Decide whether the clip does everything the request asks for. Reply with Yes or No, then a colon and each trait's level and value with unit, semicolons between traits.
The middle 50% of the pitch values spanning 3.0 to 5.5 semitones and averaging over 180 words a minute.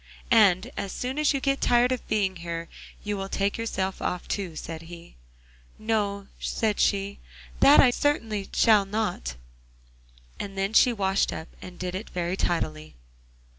No: average, 3.8 semitones; average, 160 wpm